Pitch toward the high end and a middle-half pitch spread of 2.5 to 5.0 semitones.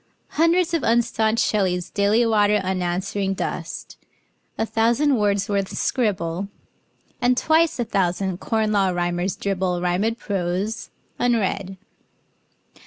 Yes: high, 205 Hz; average, 3.6 semitones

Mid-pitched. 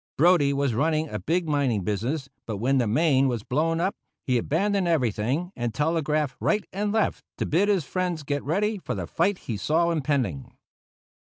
Yes: medium, 150 Hz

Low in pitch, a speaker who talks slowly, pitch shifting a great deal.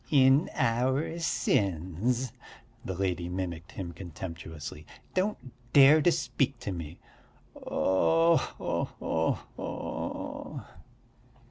Yes: low, 100 Hz; slow, 95 wpm; wide, 8.3 semitones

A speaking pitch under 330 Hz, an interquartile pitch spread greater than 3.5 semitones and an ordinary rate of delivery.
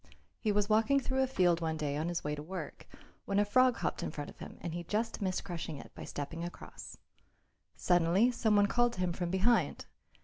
No: medium, 185 Hz; average, 4.8 semitones; fast, 225 wpm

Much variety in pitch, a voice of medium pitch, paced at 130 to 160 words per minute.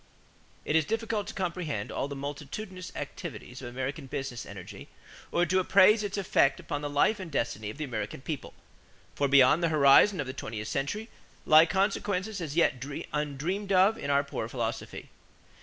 No: wide, 5.8 semitones; medium, 150 Hz; average, 175 wpm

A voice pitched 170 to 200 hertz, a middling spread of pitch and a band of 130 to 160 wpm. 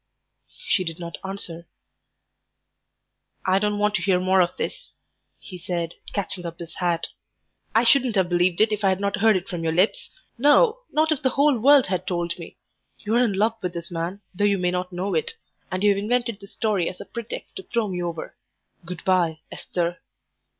No: high, 190 Hz; average, 3.5 semitones; average, 200 wpm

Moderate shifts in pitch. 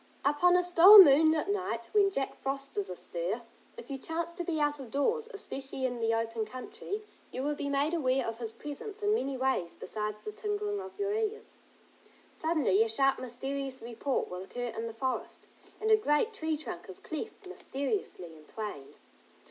No: wide, 8.2 semitones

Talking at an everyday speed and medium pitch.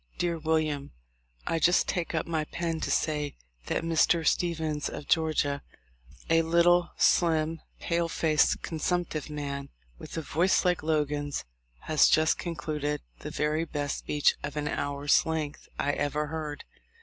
Yes: average, 145 wpm; medium, 155 Hz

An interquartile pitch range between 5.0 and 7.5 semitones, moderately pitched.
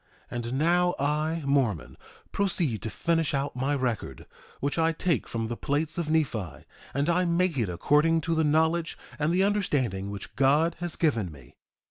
Yes: wide, 5.6 semitones; medium, 150 Hz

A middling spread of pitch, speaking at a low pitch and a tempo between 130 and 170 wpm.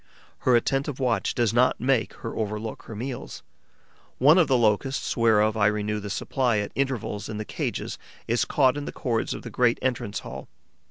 No: average, 3.5 semitones; low, 115 Hz; average, 185 wpm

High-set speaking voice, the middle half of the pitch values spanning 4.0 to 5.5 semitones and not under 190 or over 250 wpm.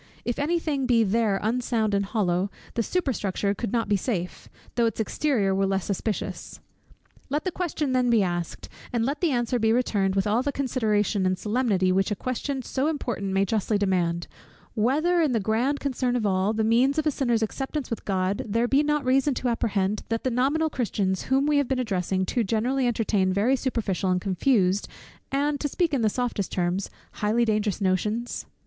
Yes: high, 230 Hz; average, 5.0 semitones; average, 195 wpm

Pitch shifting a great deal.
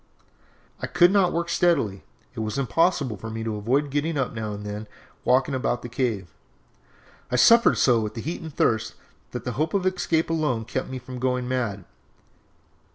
Yes: wide, 6.2 semitones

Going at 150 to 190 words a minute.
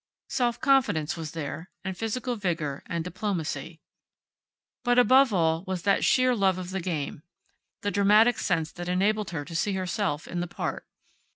Yes: average, 170 wpm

